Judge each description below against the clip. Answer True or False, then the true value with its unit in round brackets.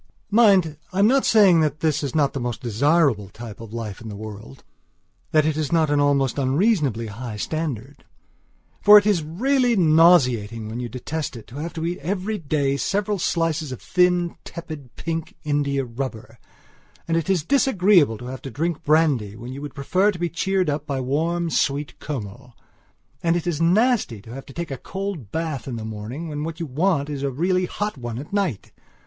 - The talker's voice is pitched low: False (150 Hz)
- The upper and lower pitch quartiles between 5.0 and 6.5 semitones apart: True (5.3 semitones)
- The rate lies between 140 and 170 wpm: False (200 wpm)